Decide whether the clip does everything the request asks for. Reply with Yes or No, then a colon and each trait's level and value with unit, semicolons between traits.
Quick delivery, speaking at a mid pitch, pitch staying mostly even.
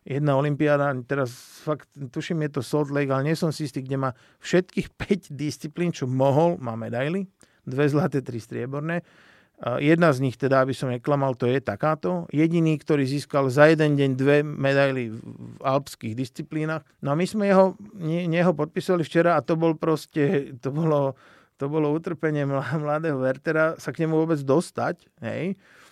No: fast, 170 wpm; medium, 150 Hz; average, 3.3 semitones